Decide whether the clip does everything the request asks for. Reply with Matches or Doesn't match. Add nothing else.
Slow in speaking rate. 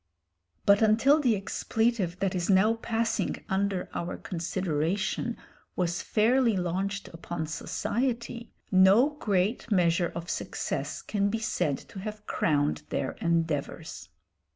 Matches